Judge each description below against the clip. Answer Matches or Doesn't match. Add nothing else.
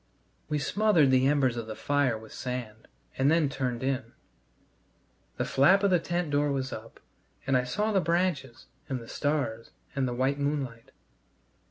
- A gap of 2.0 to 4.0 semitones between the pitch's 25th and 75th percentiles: Matches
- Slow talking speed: Doesn't match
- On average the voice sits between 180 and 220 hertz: Doesn't match